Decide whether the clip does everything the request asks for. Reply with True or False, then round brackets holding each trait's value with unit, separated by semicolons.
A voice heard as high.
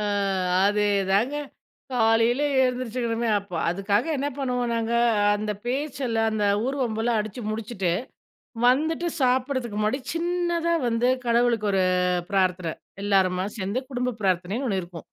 True (230 Hz)